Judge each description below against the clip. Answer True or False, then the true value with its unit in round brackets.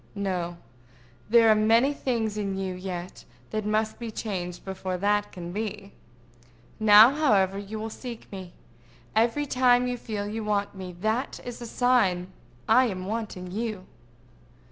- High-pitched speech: True (210 Hz)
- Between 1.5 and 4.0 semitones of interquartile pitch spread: True (3.3 semitones)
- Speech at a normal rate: True (150 wpm)